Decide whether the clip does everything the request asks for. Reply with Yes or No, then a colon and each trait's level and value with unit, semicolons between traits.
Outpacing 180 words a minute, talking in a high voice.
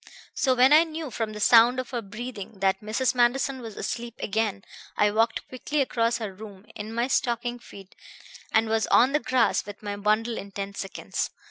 Yes: average, 195 wpm; high, 225 Hz